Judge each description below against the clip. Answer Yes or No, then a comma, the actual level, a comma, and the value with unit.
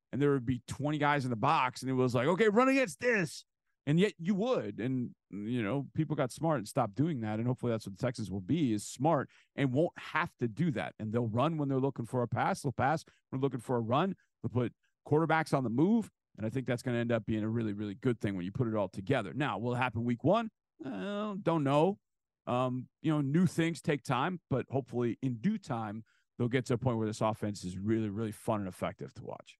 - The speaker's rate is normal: No, fast, 255 wpm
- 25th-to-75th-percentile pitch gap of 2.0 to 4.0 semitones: No, average, 5.1 semitones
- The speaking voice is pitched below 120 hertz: No, low, 130 Hz